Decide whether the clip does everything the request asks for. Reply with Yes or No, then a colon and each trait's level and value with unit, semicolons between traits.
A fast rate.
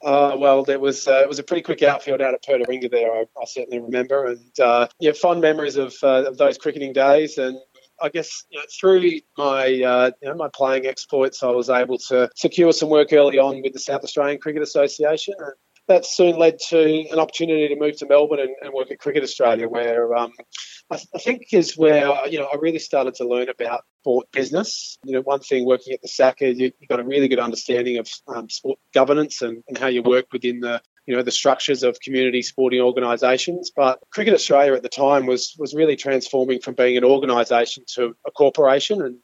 Yes: fast, 220 wpm